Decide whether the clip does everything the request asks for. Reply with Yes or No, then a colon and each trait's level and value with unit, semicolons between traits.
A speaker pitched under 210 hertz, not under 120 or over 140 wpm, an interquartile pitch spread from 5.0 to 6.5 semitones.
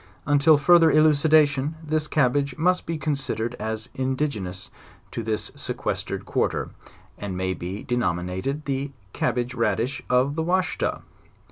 Yes: low, 135 Hz; slow, 135 wpm; wide, 5.5 semitones